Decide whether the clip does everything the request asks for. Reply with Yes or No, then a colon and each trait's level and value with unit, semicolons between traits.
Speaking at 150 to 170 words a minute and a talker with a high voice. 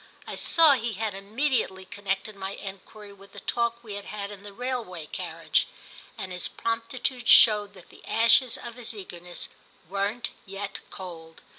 Yes: average, 160 wpm; high, 205 Hz